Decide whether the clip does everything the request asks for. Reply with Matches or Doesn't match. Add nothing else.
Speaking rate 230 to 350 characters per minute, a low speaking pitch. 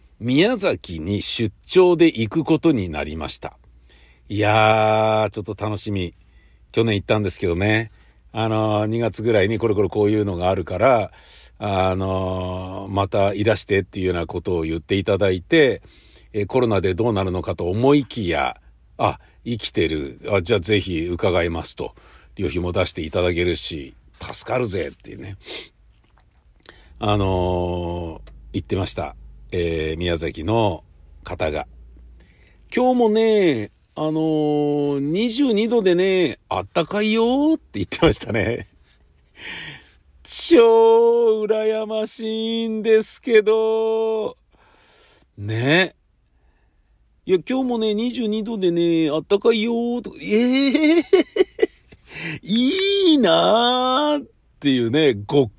Matches